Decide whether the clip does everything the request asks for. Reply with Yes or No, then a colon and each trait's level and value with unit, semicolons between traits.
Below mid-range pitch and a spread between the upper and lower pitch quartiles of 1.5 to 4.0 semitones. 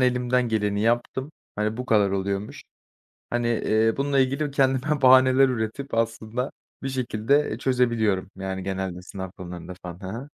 No: low, 115 Hz; average, 4.6 semitones